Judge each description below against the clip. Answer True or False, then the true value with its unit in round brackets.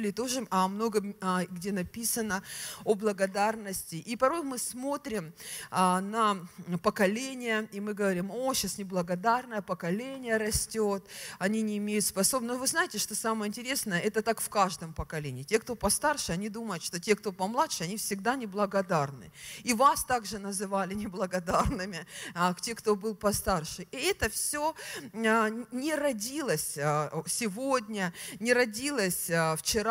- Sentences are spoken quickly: False (140 wpm)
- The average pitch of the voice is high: True (210 Hz)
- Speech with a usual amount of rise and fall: True (3.9 semitones)